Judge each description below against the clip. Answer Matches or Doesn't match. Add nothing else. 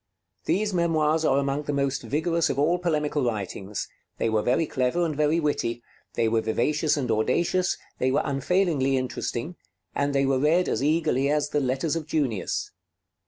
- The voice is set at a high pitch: Doesn't match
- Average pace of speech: Matches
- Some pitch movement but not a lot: Matches